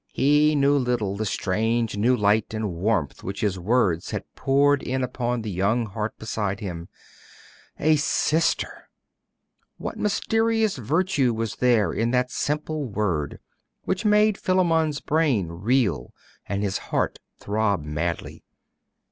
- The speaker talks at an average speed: No, slow, 130 wpm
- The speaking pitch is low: Yes, low, 115 Hz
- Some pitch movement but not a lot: No, wide, 6.2 semitones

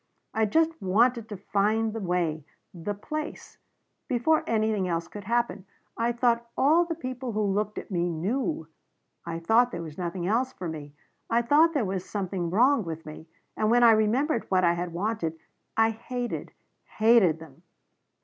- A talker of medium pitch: No, high, 215 Hz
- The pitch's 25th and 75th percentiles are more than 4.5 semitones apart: Yes, average, 5.2 semitones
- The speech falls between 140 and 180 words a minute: Yes, average, 170 wpm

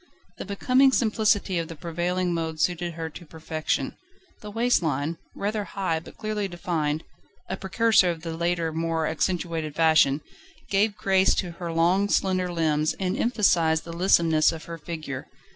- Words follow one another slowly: No, average, 160 wpm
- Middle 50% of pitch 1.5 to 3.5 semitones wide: Yes, average, 3.1 semitones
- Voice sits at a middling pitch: Yes, medium, 170 Hz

